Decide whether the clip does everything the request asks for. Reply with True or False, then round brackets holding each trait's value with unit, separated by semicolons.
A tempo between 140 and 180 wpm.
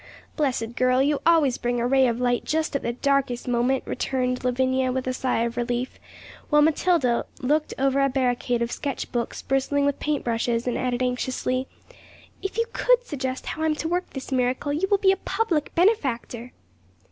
False (190 wpm)